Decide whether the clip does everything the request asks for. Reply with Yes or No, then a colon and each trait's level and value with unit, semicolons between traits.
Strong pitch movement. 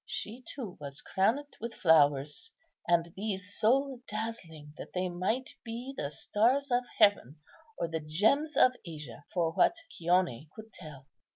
Yes: wide, 6.6 semitones